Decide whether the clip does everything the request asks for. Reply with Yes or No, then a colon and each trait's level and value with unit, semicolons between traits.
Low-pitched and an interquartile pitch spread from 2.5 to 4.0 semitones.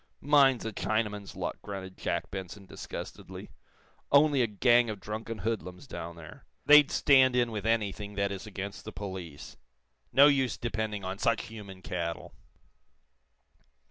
Yes: low, 105 Hz; average, 3.7 semitones